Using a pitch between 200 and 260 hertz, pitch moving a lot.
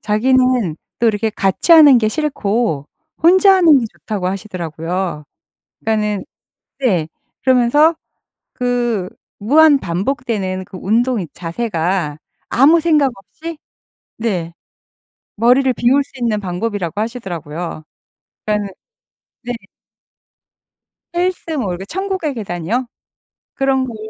Yes: high, 225 Hz; wide, 6.3 semitones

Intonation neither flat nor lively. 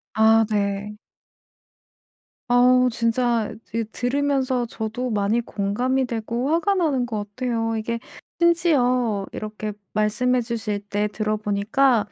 Yes: average, 3.0 semitones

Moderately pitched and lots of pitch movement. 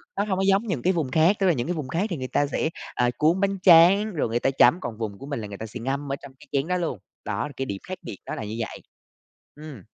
Yes: medium, 145 Hz; wide, 6.8 semitones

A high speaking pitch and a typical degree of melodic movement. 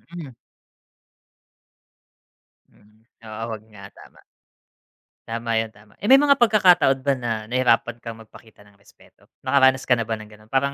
No: low, 115 Hz; average, 4.3 semitones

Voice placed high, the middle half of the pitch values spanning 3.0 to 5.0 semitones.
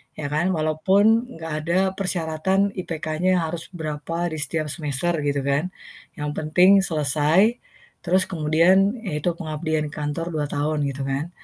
No: medium, 160 Hz; average, 3.3 semitones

